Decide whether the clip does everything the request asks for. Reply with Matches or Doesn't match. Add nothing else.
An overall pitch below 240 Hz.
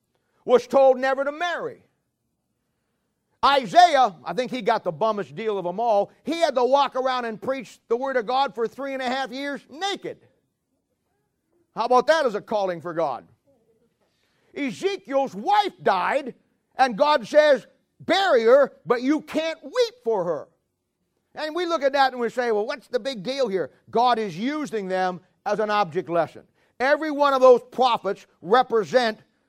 Doesn't match